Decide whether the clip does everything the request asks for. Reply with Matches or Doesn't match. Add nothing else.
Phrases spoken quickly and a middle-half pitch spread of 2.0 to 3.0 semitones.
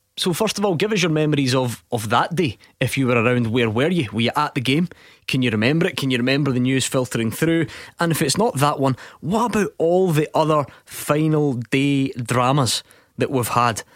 Doesn't match